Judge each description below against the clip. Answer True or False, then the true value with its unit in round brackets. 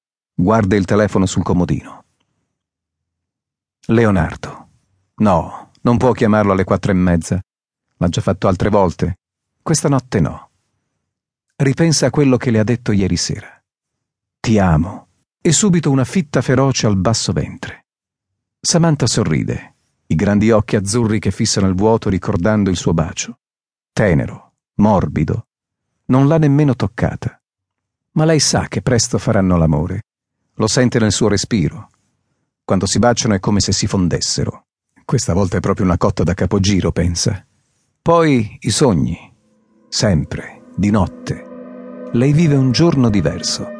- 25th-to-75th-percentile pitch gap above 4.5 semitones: True (4.9 semitones)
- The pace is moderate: True (140 wpm)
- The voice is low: True (110 Hz)